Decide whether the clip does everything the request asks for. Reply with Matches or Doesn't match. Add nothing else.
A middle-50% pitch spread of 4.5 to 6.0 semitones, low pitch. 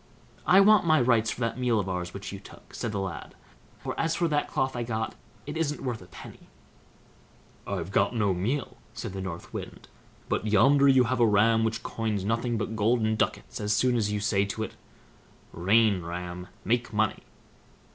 Doesn't match